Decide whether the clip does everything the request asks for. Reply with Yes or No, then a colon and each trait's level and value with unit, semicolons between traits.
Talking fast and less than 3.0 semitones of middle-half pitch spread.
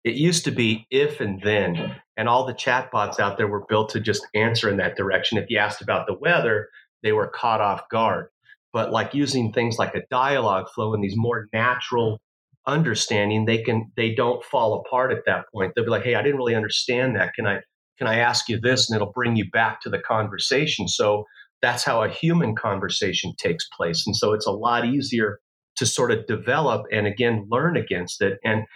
Yes: fast, 215 wpm; narrow, 2.5 semitones